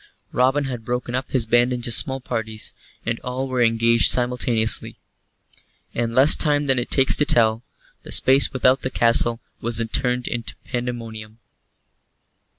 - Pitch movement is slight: Yes, narrow, 2.0 semitones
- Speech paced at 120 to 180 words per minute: Yes, average, 150 wpm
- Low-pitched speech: Yes, low, 120 Hz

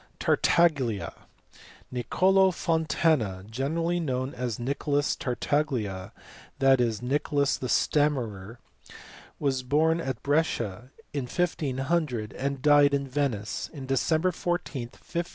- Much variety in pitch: No, average, 4.2 semitones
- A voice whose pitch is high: No, medium, 140 Hz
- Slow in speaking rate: Yes, slow, 105 wpm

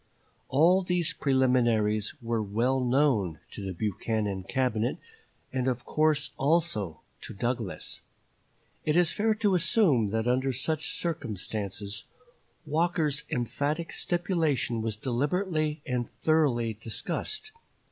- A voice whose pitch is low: Yes, low, 130 Hz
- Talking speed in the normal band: No, slow, 110 wpm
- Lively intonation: Yes, wide, 6.1 semitones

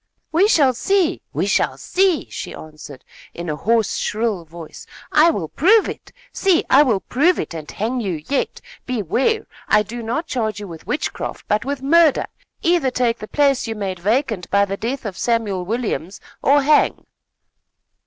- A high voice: Yes, high, 235 Hz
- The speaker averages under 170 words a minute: No, average, 175 wpm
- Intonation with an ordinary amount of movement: No, wide, 6.6 semitones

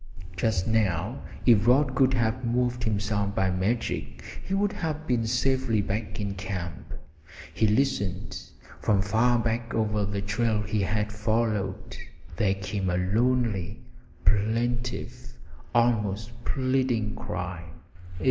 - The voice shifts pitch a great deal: No, average, 3.4 semitones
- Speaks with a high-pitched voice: No, low, 110 Hz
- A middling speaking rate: No, slow, 120 wpm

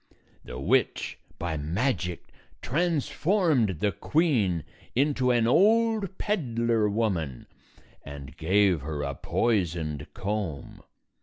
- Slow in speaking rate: Yes, slow, 95 wpm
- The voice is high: No, low, 105 Hz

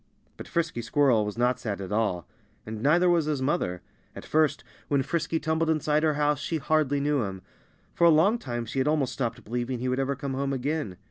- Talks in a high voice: No, medium, 140 Hz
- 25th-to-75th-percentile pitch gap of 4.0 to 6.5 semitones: Yes, average, 4.5 semitones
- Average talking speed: No, fast, 215 wpm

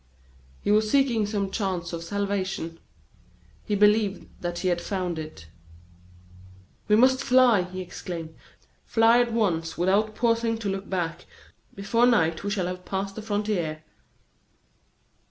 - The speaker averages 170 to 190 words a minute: No, slow, 135 wpm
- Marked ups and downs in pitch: No, average, 3.7 semitones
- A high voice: Yes, high, 200 Hz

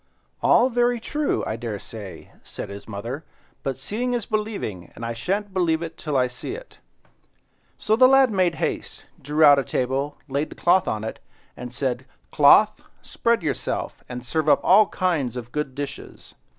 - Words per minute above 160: Yes, average, 175 wpm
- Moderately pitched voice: Yes, medium, 150 Hz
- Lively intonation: Yes, wide, 8.8 semitones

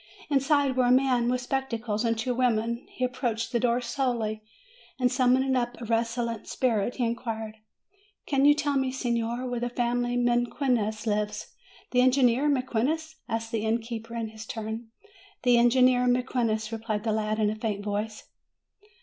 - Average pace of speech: Yes, average, 160 wpm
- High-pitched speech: Yes, high, 240 Hz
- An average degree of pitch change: No, narrow, 2.2 semitones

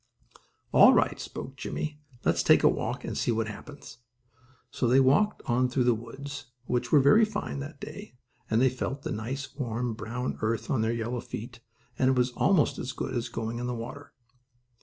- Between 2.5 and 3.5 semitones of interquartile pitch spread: Yes, average, 3.1 semitones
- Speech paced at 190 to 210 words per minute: Yes, average, 195 wpm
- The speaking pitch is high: No, low, 125 Hz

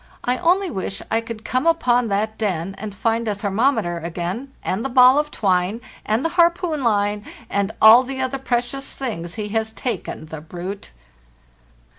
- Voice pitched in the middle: No, high, 225 Hz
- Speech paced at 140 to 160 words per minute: No, average, 170 wpm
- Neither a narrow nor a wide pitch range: Yes, average, 4.7 semitones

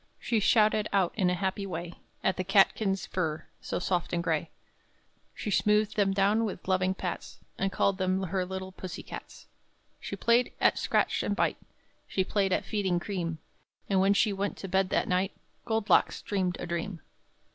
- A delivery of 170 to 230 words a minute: Yes, average, 180 wpm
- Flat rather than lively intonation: Yes, narrow, 1.8 semitones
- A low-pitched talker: No, high, 190 Hz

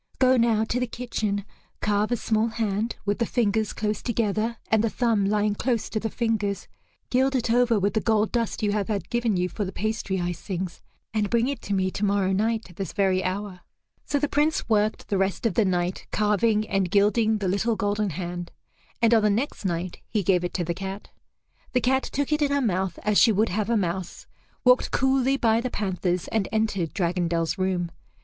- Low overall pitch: No, high, 210 Hz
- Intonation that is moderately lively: Yes, average, 3.3 semitones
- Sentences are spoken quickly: Yes, fast, 210 wpm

